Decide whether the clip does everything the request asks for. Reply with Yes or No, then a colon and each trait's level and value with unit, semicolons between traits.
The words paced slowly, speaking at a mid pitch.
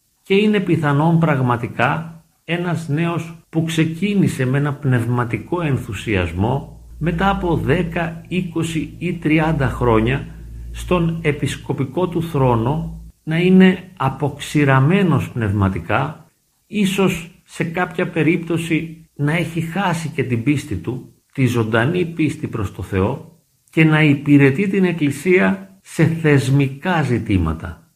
Yes: slow, 110 wpm; medium, 155 Hz